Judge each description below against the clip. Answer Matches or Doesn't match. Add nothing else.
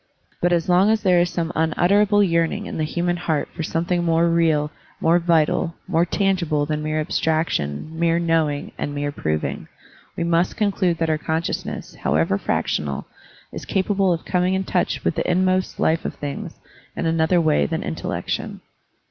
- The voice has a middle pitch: Matches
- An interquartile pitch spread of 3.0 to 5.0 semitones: Doesn't match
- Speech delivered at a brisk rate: Doesn't match